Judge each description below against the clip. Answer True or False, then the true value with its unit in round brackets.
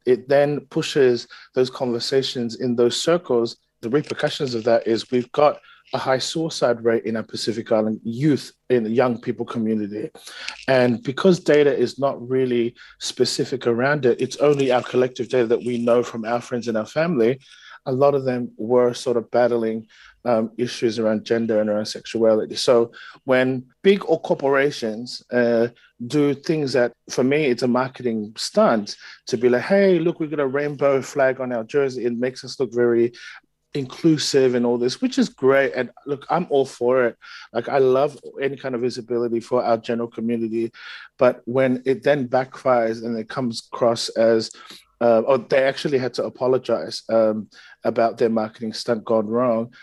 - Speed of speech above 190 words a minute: False (180 wpm)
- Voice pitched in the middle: False (125 Hz)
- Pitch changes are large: False (2.7 semitones)